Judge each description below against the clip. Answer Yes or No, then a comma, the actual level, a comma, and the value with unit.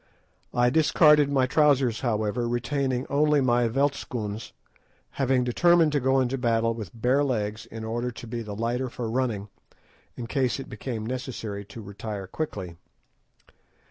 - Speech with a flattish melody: No, average, 3.3 semitones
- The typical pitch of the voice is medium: No, low, 120 Hz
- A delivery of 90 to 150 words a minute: Yes, average, 145 wpm